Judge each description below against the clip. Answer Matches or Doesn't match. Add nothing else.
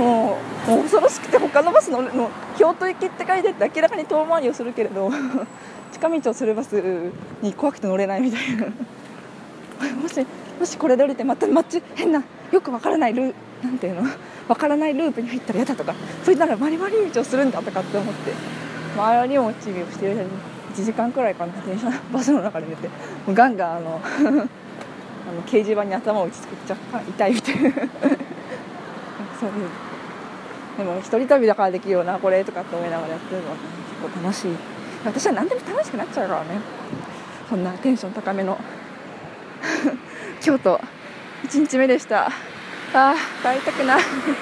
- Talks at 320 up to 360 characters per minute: Matches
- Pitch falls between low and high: Doesn't match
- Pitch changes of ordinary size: Doesn't match